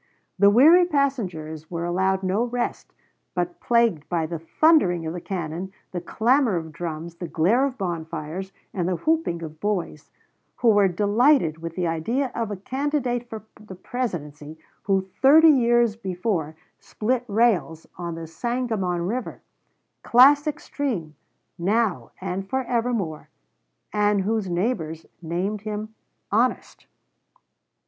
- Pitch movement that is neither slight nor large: No, wide, 6.0 semitones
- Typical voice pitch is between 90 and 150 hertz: No, high, 195 Hz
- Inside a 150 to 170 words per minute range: No, slow, 135 wpm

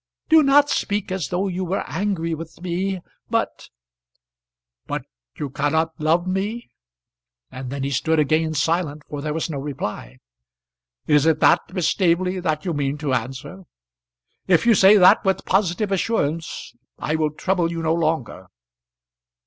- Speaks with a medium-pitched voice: Yes, medium, 165 Hz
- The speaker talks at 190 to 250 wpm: No, average, 155 wpm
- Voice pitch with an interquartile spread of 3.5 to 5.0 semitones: Yes, average, 4.2 semitones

